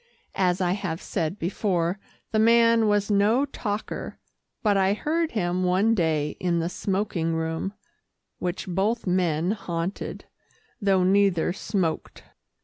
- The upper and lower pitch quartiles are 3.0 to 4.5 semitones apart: Yes, average, 3.3 semitones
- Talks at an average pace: No, slow, 130 wpm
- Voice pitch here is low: No, high, 190 Hz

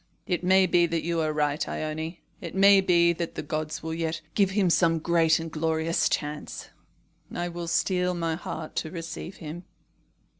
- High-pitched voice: No, medium, 165 Hz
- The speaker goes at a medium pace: Yes, average, 180 wpm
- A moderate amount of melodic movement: No, narrow, 1.7 semitones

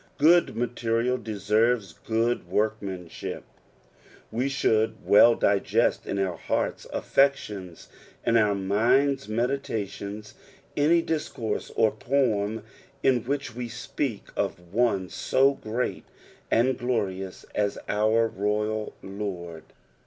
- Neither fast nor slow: No, slow, 110 wpm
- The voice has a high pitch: No, low, 110 Hz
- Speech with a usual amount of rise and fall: Yes, average, 3.5 semitones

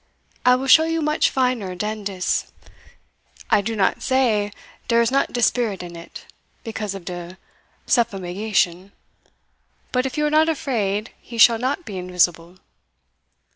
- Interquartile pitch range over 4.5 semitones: Yes, average, 5.3 semitones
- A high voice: Yes, high, 220 Hz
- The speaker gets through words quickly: No, average, 150 wpm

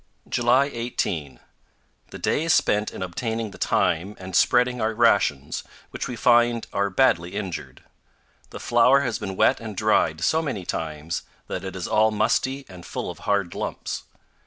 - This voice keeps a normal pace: Yes, average, 165 wpm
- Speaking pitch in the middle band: No, low, 105 Hz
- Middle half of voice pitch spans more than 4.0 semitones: Yes, average, 4.6 semitones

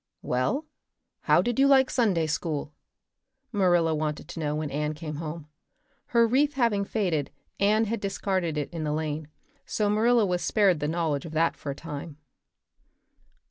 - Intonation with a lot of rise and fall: Yes, wide, 5.7 semitones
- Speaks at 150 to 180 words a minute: Yes, average, 165 wpm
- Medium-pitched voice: Yes, medium, 170 Hz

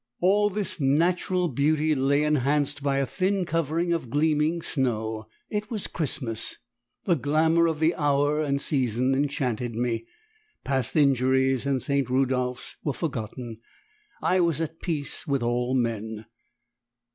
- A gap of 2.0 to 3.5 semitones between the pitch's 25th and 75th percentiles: No, average, 4.2 semitones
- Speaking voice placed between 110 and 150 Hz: Yes, medium, 140 Hz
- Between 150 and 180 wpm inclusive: No, slow, 135 wpm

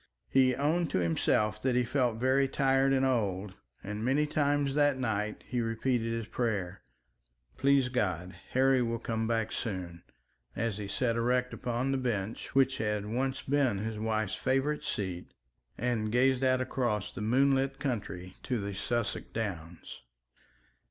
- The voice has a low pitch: Yes, low, 120 Hz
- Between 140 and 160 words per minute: Yes, average, 150 wpm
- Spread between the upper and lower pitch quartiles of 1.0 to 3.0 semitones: No, average, 4.0 semitones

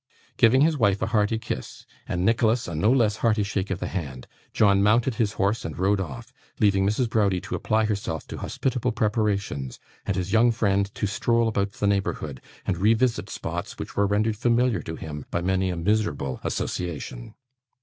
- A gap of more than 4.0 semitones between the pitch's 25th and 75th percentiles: No, average, 3.2 semitones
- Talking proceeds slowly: No, average, 185 wpm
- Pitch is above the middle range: No, low, 105 Hz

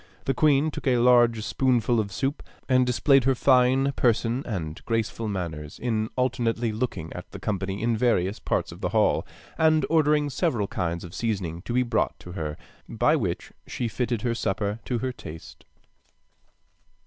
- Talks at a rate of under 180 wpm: Yes, average, 170 wpm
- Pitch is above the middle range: No, low, 115 Hz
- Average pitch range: Yes, average, 4.5 semitones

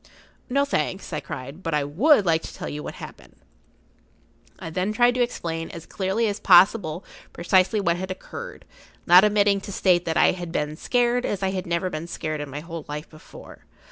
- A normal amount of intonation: Yes, average, 4.1 semitones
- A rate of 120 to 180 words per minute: No, fast, 205 wpm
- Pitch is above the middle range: No, medium, 180 Hz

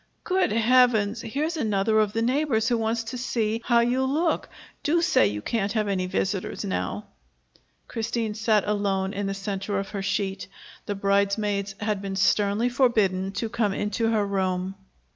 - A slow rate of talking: No, average, 165 wpm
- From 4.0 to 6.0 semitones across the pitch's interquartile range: No, average, 2.9 semitones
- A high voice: Yes, high, 210 Hz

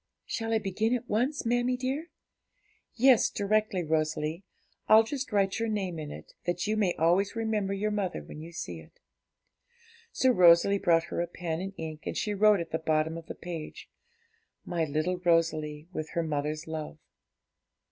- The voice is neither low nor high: Yes, medium, 180 Hz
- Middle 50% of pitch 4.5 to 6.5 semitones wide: Yes, average, 5.1 semitones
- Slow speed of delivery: No, average, 175 wpm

